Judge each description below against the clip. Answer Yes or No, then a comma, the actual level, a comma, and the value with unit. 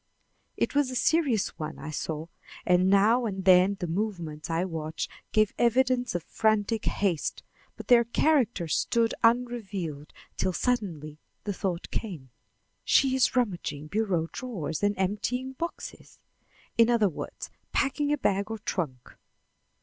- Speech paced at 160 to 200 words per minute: No, average, 140 wpm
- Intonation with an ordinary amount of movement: No, wide, 6.0 semitones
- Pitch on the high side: Yes, high, 205 Hz